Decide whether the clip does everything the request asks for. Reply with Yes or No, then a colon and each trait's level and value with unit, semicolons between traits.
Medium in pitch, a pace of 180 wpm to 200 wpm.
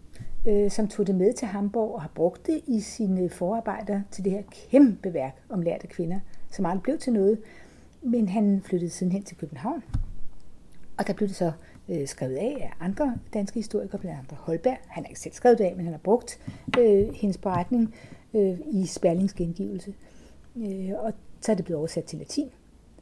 No: high, 200 Hz; average, 185 wpm